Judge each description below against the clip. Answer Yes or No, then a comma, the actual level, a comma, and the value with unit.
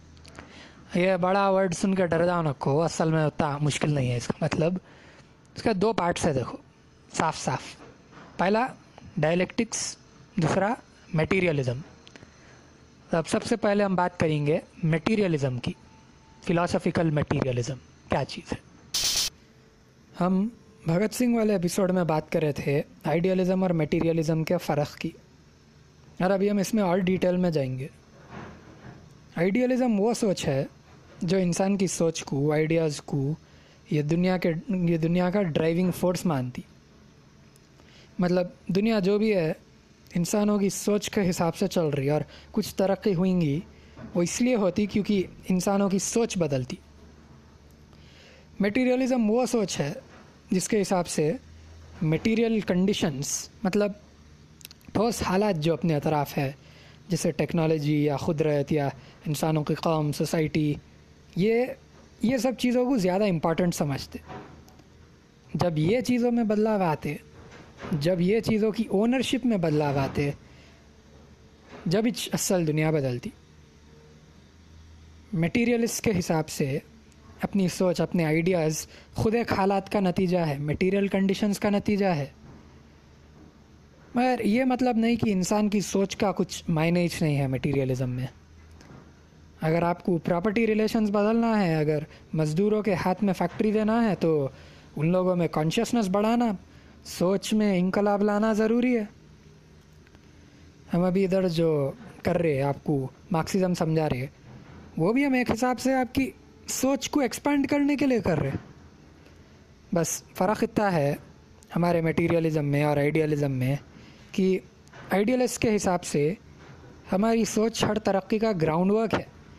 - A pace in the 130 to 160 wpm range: Yes, average, 140 wpm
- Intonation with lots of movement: Yes, wide, 6.2 semitones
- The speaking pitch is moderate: Yes, medium, 175 Hz